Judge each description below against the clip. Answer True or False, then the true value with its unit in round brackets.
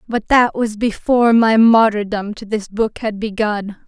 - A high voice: True (215 Hz)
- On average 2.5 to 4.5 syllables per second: True (4.3 syllables/s)